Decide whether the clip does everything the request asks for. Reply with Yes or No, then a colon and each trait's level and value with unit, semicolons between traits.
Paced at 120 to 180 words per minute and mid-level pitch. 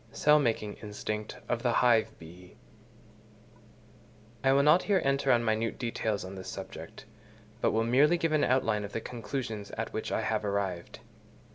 No: average, 160 wpm; low, 110 Hz